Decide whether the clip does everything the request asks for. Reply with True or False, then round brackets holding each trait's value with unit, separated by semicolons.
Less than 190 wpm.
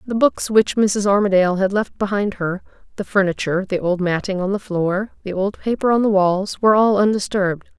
False (200 wpm)